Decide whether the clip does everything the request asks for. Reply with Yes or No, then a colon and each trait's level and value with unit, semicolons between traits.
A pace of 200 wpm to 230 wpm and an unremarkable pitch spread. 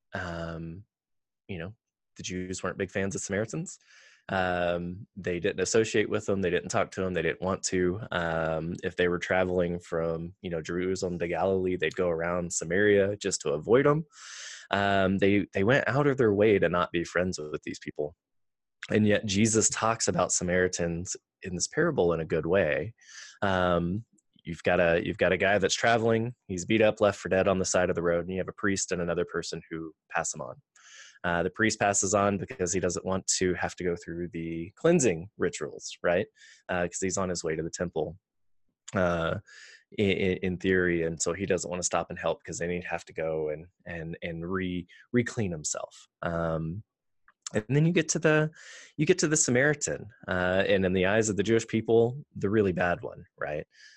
Yes: fast, 205 wpm; average, 3.4 semitones